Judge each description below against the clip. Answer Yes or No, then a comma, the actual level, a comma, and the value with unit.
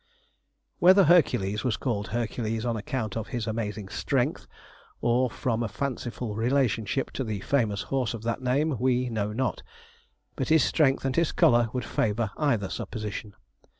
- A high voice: No, low, 120 Hz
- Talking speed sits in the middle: Yes, average, 155 wpm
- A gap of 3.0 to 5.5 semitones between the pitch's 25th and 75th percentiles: Yes, average, 3.5 semitones